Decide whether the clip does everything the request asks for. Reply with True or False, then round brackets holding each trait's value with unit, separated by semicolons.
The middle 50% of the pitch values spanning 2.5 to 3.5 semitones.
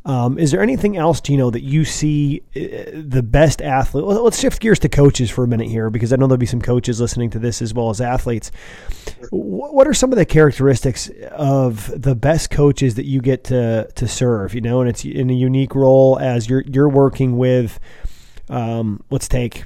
True (3.0 semitones)